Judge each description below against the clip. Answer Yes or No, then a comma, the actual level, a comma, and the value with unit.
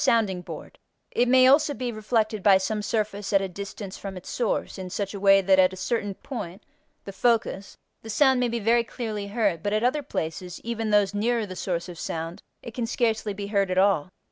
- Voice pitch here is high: Yes, high, 205 Hz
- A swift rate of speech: Yes, fast, 220 wpm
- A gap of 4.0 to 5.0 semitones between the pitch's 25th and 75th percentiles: No, average, 3.2 semitones